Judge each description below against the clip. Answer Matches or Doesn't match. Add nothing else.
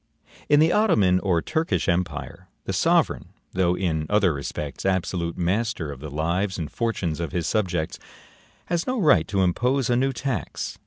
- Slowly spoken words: Doesn't match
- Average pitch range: Doesn't match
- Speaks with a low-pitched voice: Matches